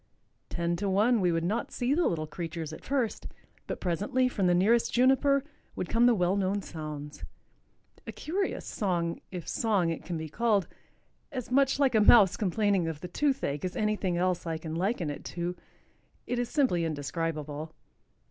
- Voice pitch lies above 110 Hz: Yes, medium, 185 Hz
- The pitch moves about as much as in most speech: No, wide, 6.1 semitones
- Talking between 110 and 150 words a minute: No, average, 170 wpm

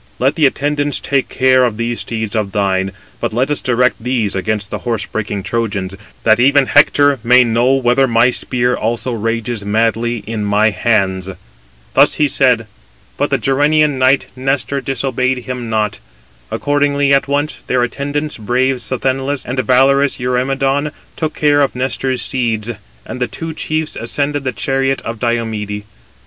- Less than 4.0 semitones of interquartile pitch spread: Yes, average, 3.3 semitones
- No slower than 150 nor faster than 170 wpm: Yes, average, 160 wpm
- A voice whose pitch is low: Yes, low, 125 Hz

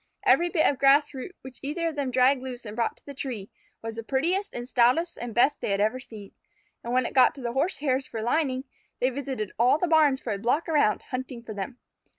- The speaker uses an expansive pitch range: No, average, 3.4 semitones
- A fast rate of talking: Yes, fast, 235 wpm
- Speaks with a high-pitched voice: Yes, very high, 260 Hz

